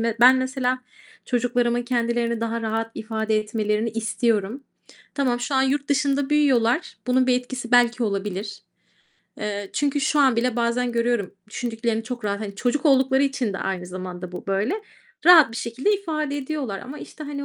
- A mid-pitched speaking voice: No, high, 240 Hz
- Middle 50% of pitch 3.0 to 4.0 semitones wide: Yes, average, 3.3 semitones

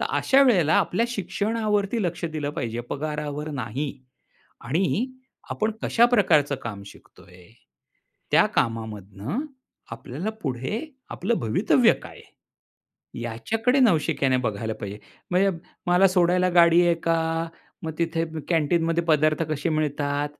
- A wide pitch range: Yes, wide, 6.0 semitones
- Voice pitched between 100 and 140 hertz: No, medium, 160 Hz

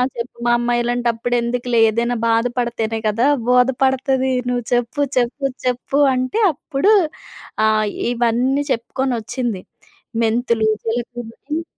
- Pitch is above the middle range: Yes, high, 245 Hz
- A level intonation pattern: Yes, narrow, 1.7 semitones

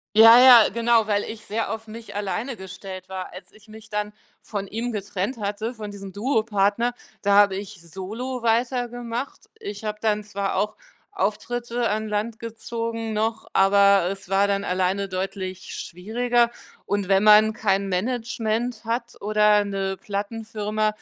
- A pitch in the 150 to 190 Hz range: No, high, 210 Hz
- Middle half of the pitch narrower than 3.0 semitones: Yes, narrow, 2.5 semitones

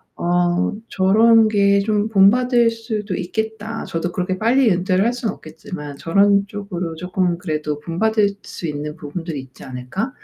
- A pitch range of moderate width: Yes, average, 4.4 semitones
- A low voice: No, high, 195 Hz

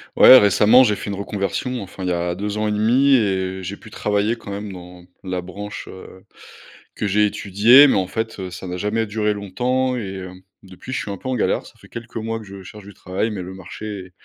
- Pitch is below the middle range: Yes, low, 100 Hz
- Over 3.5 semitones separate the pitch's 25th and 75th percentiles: No, average, 2.8 semitones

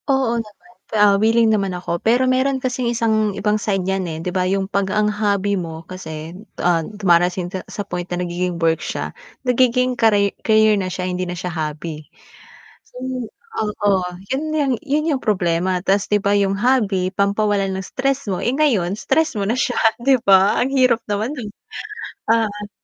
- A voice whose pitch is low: No, high, 205 Hz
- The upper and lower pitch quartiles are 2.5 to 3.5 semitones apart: No, average, 4.1 semitones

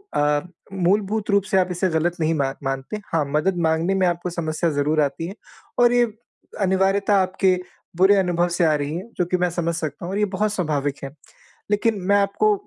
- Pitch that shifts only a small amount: No, average, 3.9 semitones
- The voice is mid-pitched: Yes, medium, 180 Hz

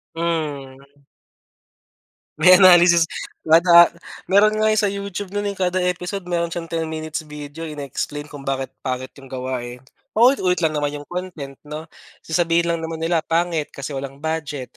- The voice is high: No, medium, 165 Hz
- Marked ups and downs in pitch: No, average, 3.6 semitones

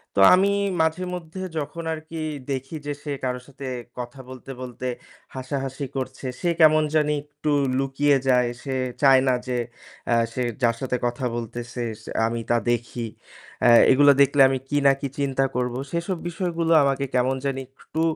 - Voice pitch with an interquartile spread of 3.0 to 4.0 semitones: Yes, average, 3.3 semitones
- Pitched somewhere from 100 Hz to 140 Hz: Yes, low, 135 Hz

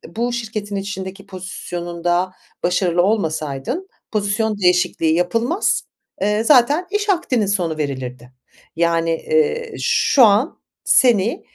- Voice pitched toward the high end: Yes, high, 200 Hz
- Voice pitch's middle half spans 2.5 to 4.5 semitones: No, wide, 5.5 semitones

